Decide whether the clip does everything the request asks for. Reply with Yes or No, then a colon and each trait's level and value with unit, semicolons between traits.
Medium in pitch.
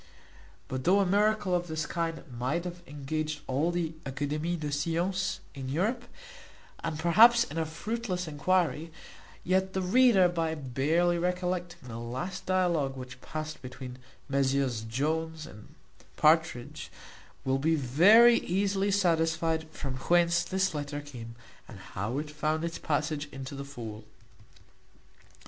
Yes: medium, 160 Hz